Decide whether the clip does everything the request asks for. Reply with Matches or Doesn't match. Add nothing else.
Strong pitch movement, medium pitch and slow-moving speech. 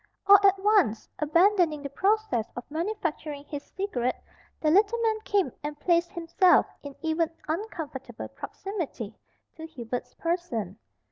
Doesn't match